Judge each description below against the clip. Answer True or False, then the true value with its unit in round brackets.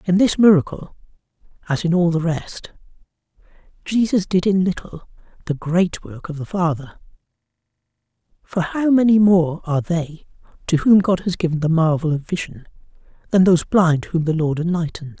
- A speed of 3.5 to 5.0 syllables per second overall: False (5.2 syllables/s)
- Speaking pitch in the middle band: True (170 Hz)